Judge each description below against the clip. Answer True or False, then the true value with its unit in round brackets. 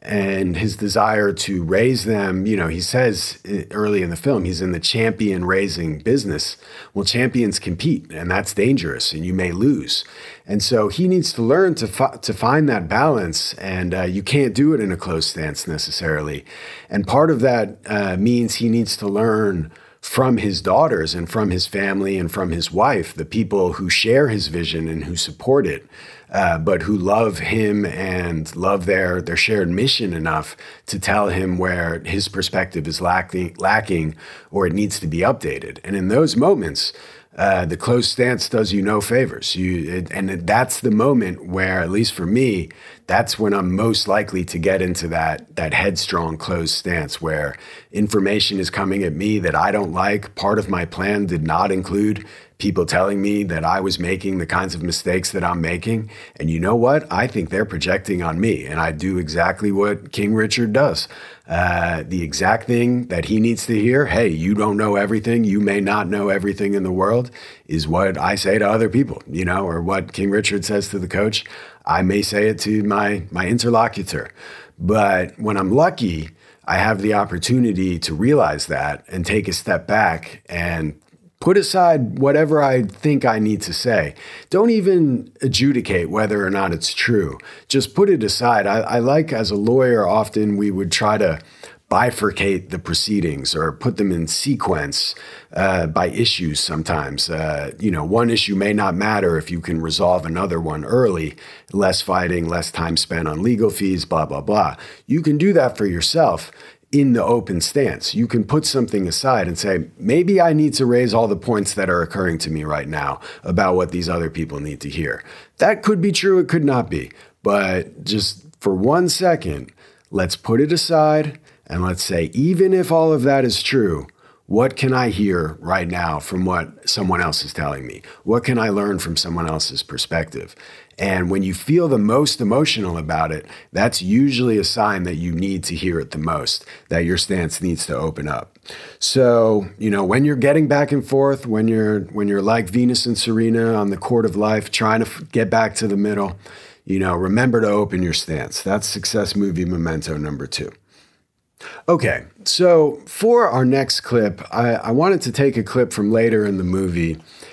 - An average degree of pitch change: True (4.6 semitones)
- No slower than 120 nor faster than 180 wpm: False (195 wpm)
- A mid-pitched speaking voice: False (100 Hz)